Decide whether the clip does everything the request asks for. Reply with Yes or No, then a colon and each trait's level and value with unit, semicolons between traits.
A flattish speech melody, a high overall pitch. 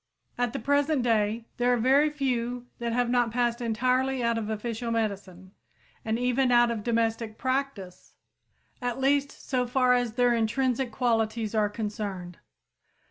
Yes: narrow, 2.2 semitones; high, 235 Hz